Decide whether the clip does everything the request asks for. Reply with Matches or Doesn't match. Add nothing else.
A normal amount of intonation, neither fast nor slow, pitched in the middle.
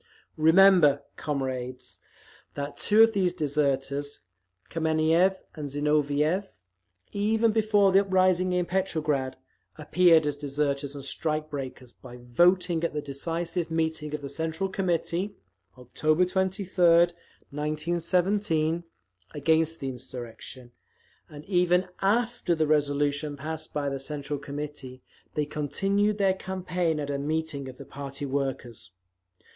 Doesn't match